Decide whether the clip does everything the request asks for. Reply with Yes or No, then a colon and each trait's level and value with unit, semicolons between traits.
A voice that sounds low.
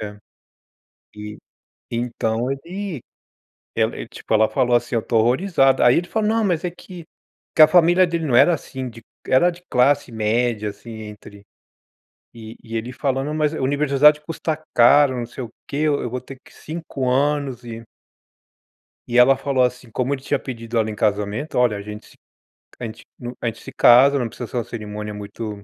Yes: low, 125 Hz